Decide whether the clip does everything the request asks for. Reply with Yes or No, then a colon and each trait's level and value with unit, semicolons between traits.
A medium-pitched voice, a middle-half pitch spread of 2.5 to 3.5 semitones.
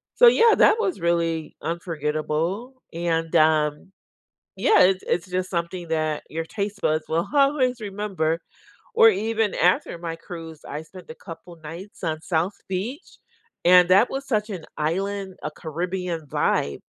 No: medium, 175 Hz; average, 3.9 semitones